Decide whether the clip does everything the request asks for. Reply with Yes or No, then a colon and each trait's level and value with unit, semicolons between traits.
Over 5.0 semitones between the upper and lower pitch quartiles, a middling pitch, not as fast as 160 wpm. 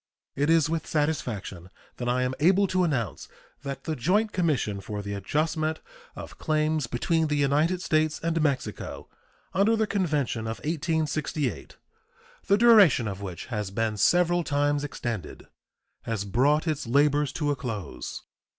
Yes: wide, 5.4 semitones; medium, 150 Hz; average, 150 wpm